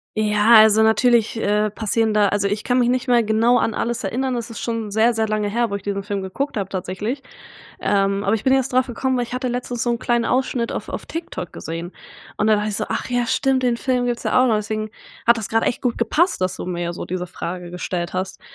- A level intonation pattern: No, average, 3.3 semitones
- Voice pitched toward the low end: No, high, 220 Hz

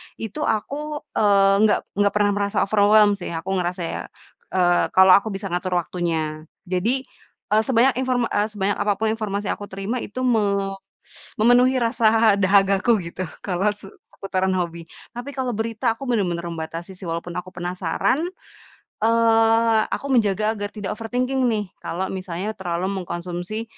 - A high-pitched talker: Yes, high, 205 Hz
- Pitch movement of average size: Yes, average, 3.4 semitones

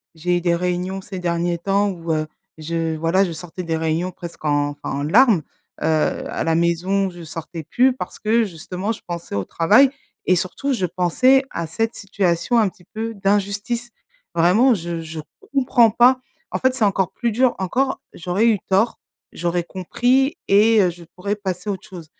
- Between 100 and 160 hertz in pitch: No, medium, 185 Hz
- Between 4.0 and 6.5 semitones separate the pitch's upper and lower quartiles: Yes, average, 4.6 semitones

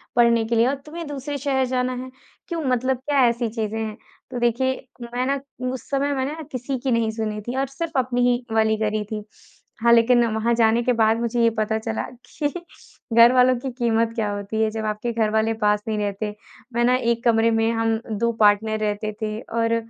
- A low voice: No, high, 230 Hz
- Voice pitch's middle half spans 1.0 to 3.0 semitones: Yes, narrow, 2.5 semitones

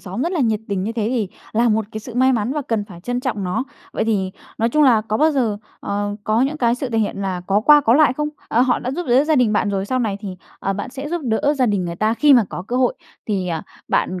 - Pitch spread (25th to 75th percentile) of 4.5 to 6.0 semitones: No, average, 4.1 semitones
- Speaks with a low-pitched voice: No, high, 225 Hz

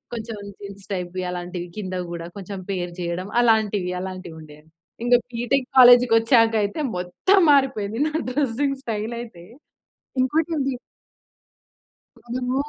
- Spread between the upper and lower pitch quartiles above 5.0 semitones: Yes, wide, 5.4 semitones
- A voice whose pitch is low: No, high, 215 Hz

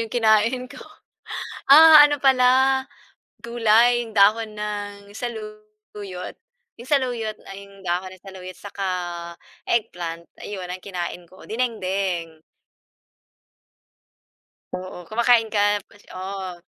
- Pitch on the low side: No, high, 210 Hz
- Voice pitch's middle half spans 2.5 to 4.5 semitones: Yes, average, 3.9 semitones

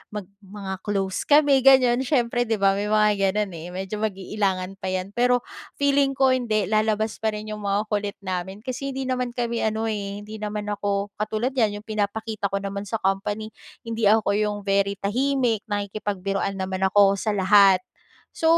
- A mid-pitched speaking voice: No, high, 210 Hz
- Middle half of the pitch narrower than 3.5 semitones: Yes, narrow, 2.5 semitones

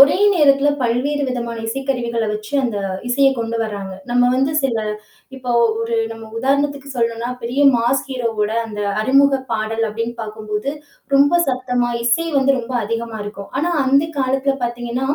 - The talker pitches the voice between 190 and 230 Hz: No, high, 245 Hz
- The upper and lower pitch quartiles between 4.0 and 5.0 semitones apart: No, average, 3.0 semitones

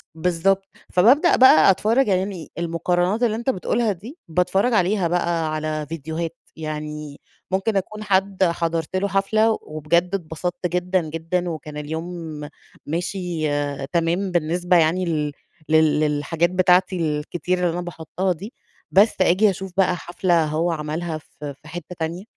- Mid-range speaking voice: Yes, medium, 175 Hz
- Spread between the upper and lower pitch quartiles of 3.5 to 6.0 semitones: No, average, 3.1 semitones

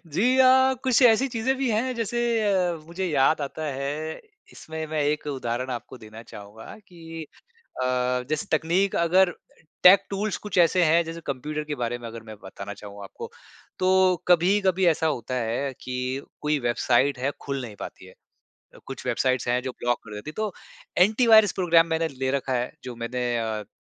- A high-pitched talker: No, medium, 155 Hz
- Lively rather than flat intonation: Yes, wide, 6.9 semitones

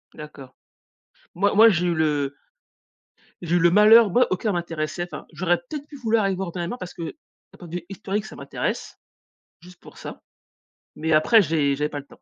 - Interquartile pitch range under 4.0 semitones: No, average, 4.6 semitones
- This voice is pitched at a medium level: Yes, medium, 175 Hz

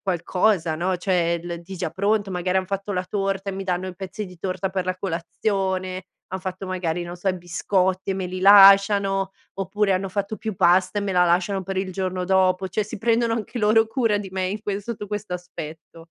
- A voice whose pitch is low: No, high, 190 Hz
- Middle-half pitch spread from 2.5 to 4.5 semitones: No, narrow, 1.8 semitones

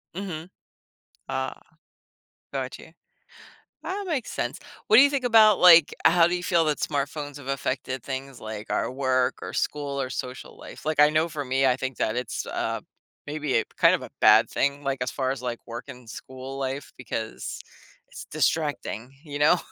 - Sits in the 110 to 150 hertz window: Yes, medium, 140 Hz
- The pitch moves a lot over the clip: No, average, 3.7 semitones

